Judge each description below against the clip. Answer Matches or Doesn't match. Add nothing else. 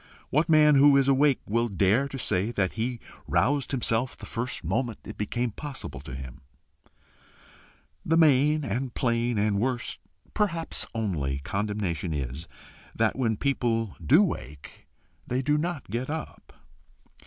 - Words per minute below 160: Matches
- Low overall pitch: Matches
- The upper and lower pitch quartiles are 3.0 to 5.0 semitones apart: Doesn't match